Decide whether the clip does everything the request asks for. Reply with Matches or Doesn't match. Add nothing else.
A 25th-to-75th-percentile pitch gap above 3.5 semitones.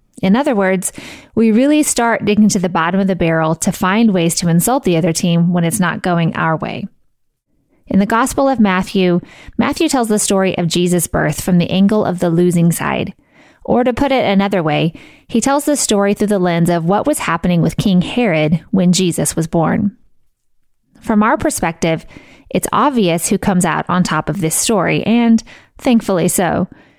Matches